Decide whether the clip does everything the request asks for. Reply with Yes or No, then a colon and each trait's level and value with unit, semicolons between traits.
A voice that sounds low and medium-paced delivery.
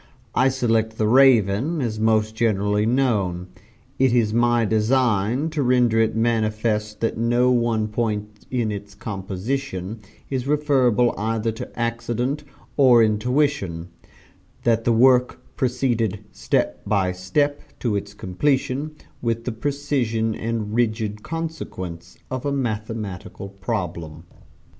No: low, 115 Hz; slow, 120 wpm